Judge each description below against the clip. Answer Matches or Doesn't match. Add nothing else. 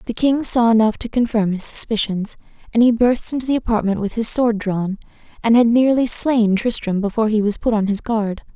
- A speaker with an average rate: Doesn't match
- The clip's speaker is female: Matches